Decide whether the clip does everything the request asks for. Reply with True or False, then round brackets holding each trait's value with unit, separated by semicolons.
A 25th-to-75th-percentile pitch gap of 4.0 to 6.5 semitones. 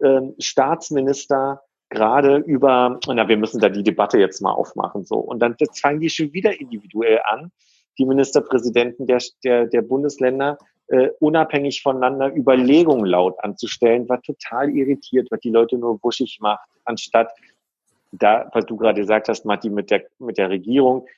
False (3.3 semitones)